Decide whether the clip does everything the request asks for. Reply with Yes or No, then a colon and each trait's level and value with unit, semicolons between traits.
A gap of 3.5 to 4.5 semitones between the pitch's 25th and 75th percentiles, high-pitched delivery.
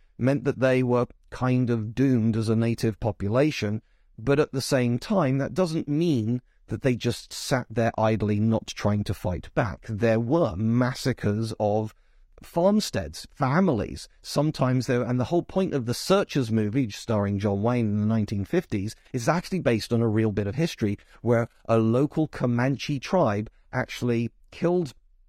No: average, 4.2 semitones; low, 120 Hz